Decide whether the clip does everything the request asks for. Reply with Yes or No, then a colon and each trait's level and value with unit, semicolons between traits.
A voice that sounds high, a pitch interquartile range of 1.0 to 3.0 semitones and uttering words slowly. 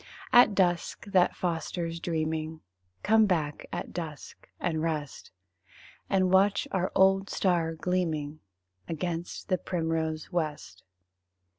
No: medium, 170 Hz; average, 2.7 semitones; slow, 110 wpm